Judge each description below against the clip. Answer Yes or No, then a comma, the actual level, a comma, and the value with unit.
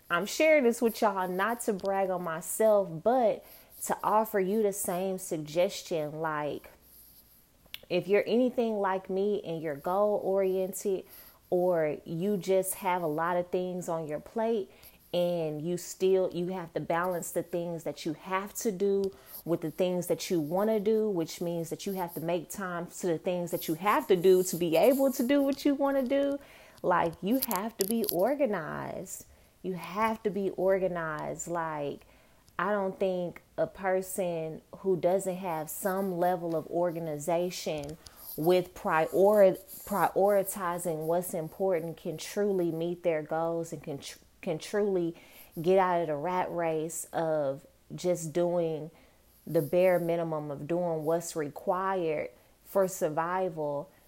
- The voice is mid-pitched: Yes, medium, 180 Hz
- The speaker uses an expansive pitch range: No, average, 2.9 semitones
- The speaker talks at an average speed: Yes, average, 160 wpm